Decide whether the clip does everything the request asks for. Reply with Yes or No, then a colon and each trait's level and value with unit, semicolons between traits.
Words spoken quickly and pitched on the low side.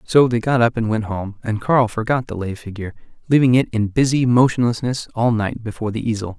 Yes: fast, 215 wpm; low, 115 Hz